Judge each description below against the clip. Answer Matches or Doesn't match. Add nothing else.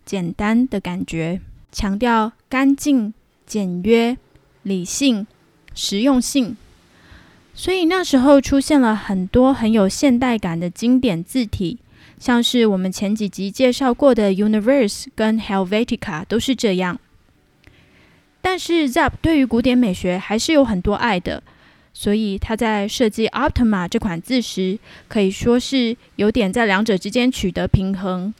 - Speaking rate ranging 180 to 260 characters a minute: Matches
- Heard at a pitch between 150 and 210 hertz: Doesn't match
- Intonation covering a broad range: Doesn't match